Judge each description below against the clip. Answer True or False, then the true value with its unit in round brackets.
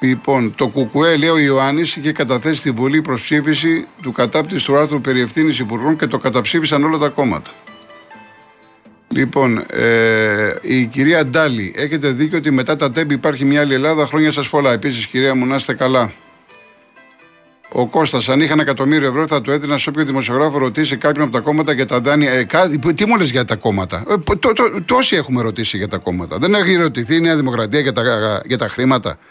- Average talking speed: False (200 wpm)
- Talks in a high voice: False (140 Hz)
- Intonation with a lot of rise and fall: False (3.4 semitones)